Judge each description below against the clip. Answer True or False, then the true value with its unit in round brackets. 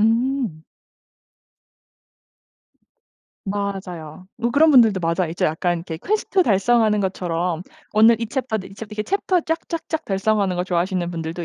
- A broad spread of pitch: False (5.0 semitones)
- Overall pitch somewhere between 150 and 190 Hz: False (200 Hz)